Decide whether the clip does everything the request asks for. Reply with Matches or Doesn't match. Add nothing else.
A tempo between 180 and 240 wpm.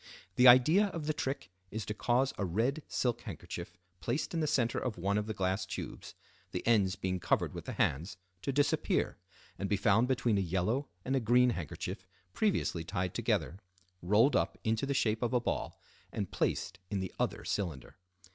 Matches